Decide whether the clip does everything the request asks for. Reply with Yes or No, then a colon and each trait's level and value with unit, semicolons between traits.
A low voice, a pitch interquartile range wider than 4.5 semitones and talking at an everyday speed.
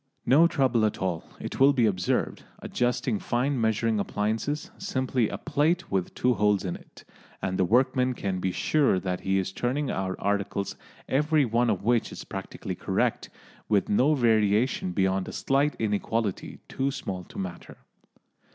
Yes: low, 115 Hz; average, 5.2 semitones; average, 160 wpm